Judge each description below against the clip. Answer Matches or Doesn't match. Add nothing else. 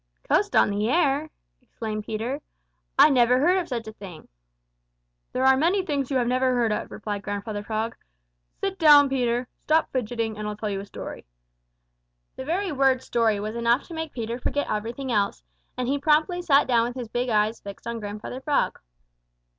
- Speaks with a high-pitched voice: Matches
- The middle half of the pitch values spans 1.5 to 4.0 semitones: Doesn't match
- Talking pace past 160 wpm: Matches